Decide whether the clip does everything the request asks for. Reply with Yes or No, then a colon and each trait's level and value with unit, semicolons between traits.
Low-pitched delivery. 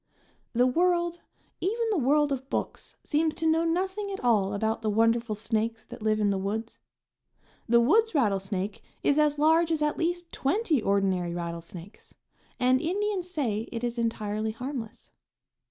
No: very high, 250 Hz